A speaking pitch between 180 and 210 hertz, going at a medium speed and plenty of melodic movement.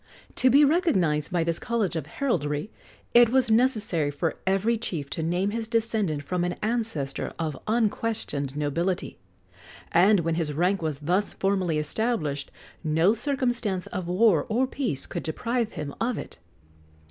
Yes: high, 190 Hz; average, 150 wpm; wide, 6.4 semitones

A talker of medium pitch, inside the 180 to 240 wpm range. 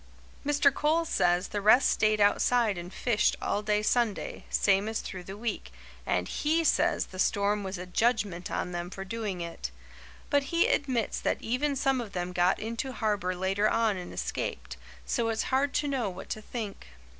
No: high, 215 Hz; average, 185 wpm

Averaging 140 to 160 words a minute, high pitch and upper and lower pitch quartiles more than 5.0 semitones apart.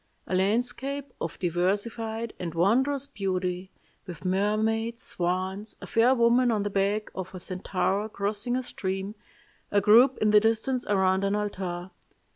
No: average, 145 wpm; high, 205 Hz; average, 3.5 semitones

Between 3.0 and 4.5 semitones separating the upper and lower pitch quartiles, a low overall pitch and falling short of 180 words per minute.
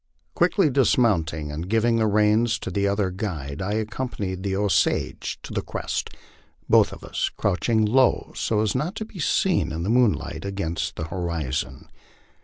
No: average, 5.1 semitones; low, 105 Hz; average, 165 wpm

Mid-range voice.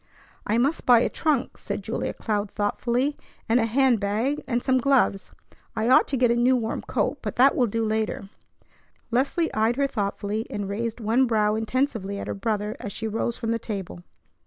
No: high, 230 Hz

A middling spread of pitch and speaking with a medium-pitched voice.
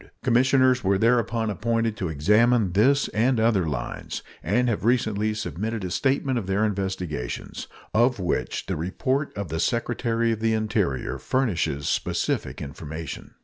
No: average, 4.4 semitones; low, 110 Hz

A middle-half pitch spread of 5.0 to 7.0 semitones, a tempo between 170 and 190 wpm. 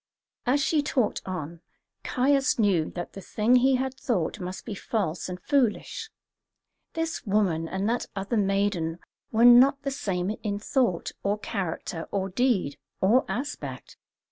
No: wide, 5.4 semitones; average, 145 wpm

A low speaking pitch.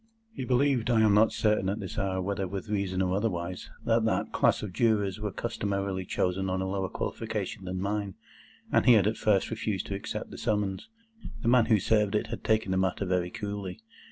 Yes: low, 100 Hz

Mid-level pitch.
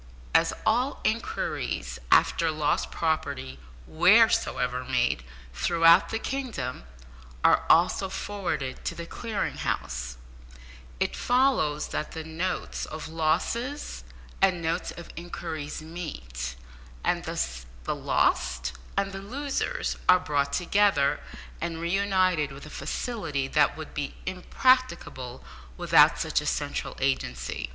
Yes: medium, 160 Hz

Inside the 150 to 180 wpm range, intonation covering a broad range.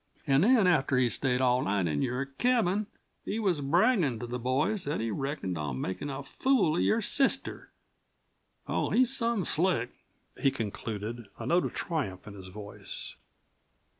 Yes: average, 165 wpm; wide, 8.5 semitones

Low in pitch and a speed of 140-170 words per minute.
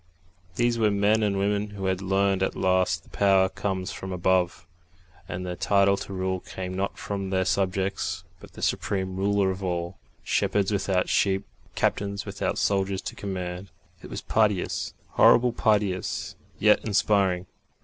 Yes: very low, 95 Hz; average, 160 wpm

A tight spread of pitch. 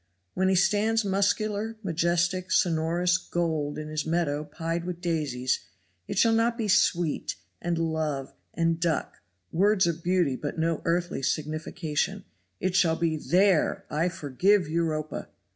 No: average, 3.1 semitones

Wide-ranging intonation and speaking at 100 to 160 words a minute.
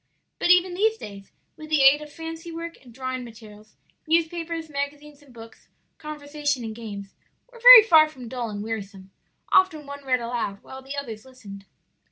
No: wide, 6.0 semitones; average, 175 wpm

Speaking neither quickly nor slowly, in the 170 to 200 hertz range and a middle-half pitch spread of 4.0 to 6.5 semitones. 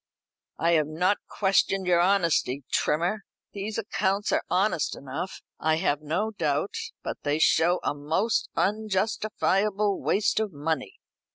No: slow, 130 wpm; medium, 185 Hz; average, 4.6 semitones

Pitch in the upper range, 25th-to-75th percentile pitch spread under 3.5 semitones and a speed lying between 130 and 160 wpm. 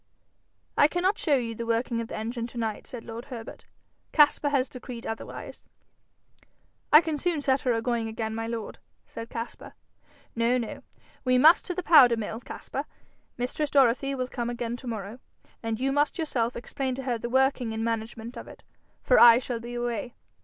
No: high, 240 Hz; average, 2.7 semitones; average, 185 wpm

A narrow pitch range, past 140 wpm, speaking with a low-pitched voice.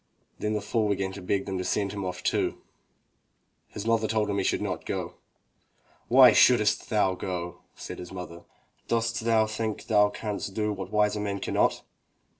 Yes: narrow, 2.2 semitones; average, 180 wpm; low, 105 Hz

